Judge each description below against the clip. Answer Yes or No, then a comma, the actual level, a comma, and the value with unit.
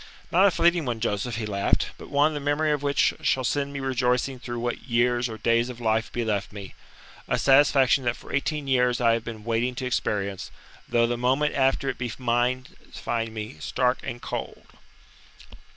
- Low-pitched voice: Yes, low, 125 Hz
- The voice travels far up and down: No, average, 2.7 semitones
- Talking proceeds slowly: No, average, 195 wpm